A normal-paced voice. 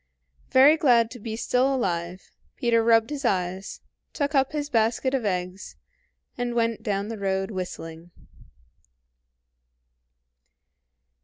No: slow, 120 wpm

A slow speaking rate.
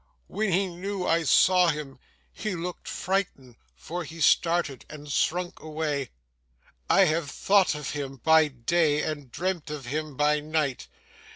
No: average, 150 wpm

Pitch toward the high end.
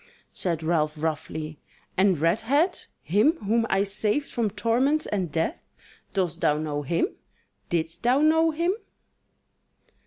Yes: high, 195 Hz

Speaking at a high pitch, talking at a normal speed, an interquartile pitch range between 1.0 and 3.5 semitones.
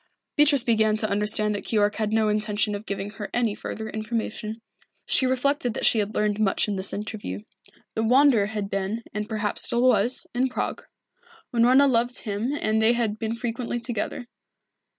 Yes: high, 220 Hz; average, 175 wpm; narrow, 2.4 semitones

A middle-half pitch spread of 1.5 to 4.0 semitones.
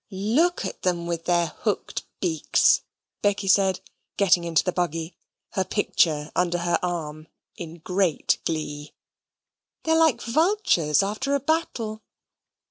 No: average, 4.5 semitones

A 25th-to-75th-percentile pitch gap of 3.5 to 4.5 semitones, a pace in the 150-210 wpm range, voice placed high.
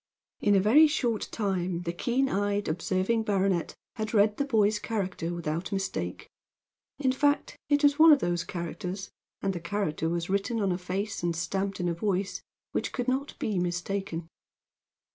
Yes: average, 4.0 semitones; average, 170 wpm; high, 195 Hz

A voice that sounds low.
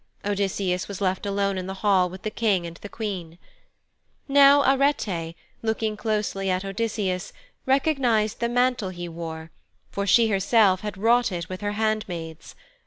No: high, 200 Hz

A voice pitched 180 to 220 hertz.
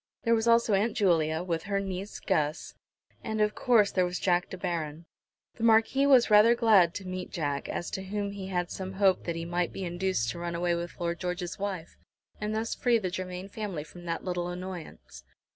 Yes: medium, 185 Hz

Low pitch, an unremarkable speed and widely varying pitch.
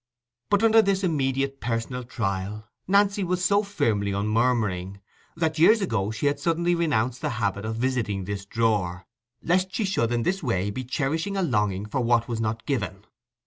Yes: low, 120 Hz; average, 175 wpm; wide, 8.1 semitones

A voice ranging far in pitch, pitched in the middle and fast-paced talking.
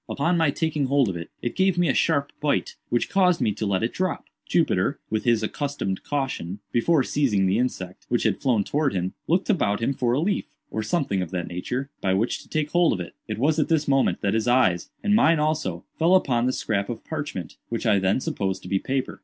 No: wide, 7.3 semitones; low, 130 Hz; fast, 235 wpm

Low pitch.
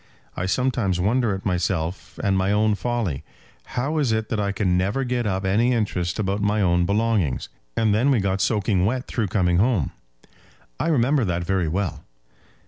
Yes: low, 100 Hz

